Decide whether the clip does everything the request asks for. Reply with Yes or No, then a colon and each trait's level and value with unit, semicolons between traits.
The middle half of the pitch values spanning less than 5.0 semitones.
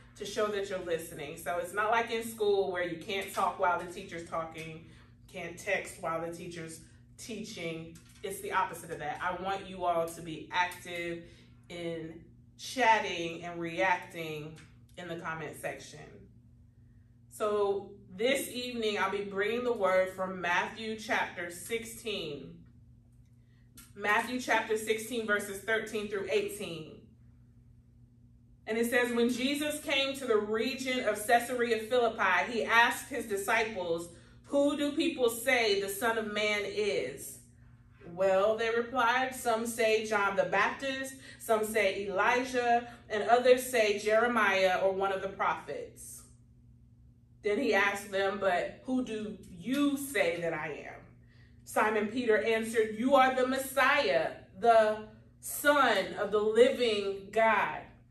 No: average, 5.3 semitones